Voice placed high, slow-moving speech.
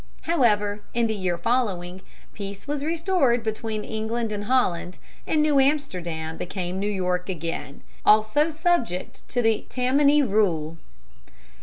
Yes: high, 215 Hz; slow, 130 wpm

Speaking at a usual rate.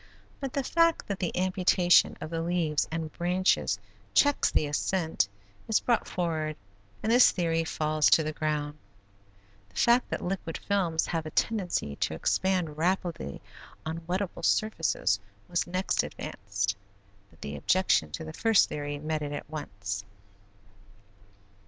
Yes: average, 145 wpm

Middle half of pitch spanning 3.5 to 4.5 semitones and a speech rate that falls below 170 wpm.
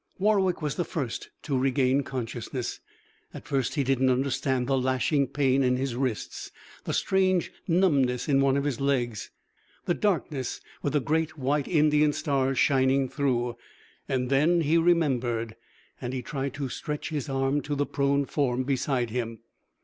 No: narrow, 2.5 semitones; average, 155 wpm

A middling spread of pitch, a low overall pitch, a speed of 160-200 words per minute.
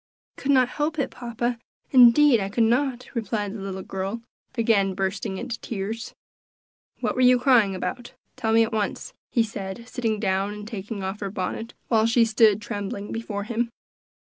No: average, 3.1 semitones; high, 225 Hz; average, 175 wpm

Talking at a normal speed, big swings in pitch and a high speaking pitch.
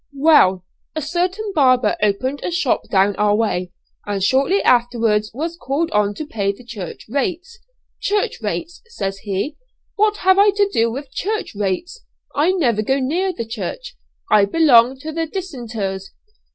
Yes: average, 160 wpm; wide, 8.6 semitones; very high, 260 Hz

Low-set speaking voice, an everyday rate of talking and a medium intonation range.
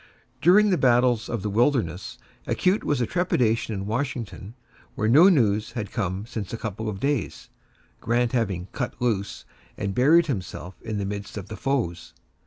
Yes: low, 115 Hz; average, 170 wpm; average, 4.1 semitones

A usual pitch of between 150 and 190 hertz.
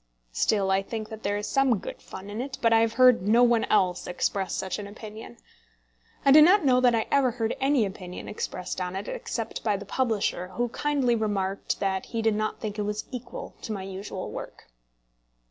No: high, 215 Hz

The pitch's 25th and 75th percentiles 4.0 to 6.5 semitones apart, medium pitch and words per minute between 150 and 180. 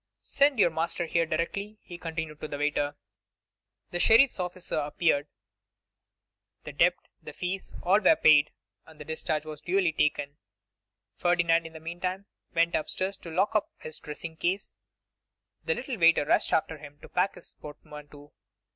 No: average, 3.2 semitones; medium, 165 Hz; average, 155 wpm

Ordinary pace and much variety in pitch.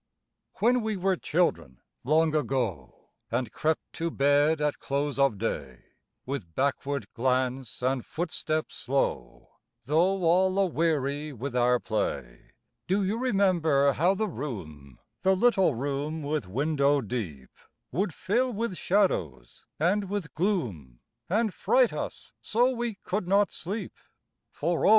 No: slow, 130 wpm; wide, 7.0 semitones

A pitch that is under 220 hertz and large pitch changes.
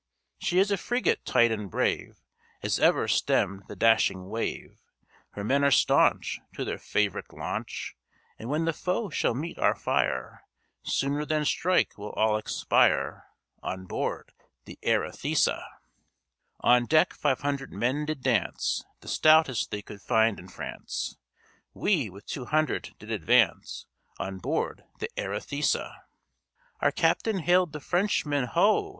Yes: medium, 140 Hz; wide, 6.7 semitones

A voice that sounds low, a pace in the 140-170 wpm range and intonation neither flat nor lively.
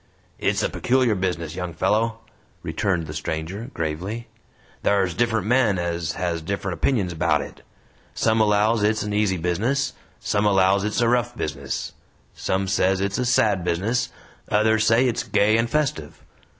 Yes: low, 100 Hz; average, 155 wpm; average, 4.5 semitones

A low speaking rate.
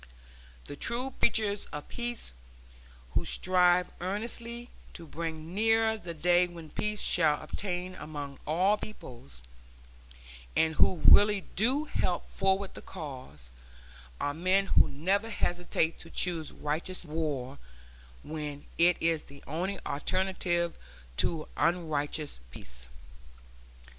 Yes: slow, 115 wpm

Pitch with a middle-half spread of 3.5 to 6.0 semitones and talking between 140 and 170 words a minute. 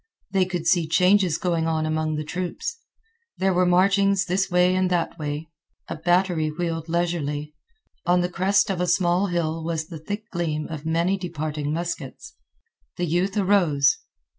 No: average, 2.7 semitones; average, 165 wpm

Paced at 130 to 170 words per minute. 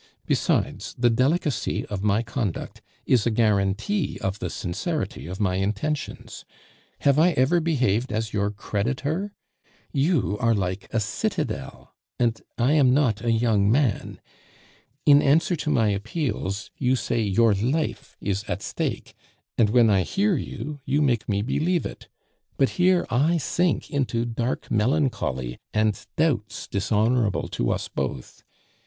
Yes: average, 145 wpm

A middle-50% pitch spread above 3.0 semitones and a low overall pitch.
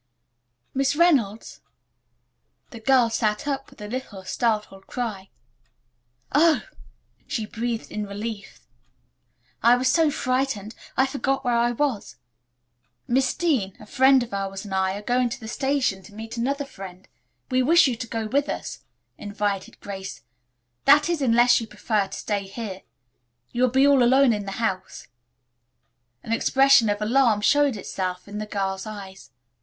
No: average, 4.7 semitones; high, 230 Hz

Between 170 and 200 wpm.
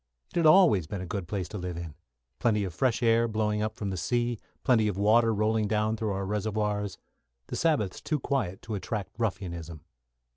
Yes: average, 195 wpm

